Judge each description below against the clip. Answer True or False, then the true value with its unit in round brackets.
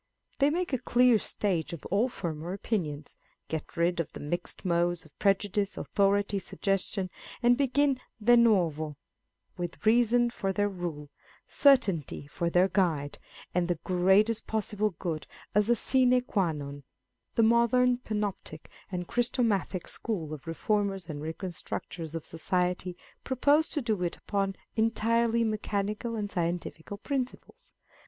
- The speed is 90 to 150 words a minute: True (140 wpm)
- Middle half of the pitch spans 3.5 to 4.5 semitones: False (5.2 semitones)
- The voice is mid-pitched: False (200 Hz)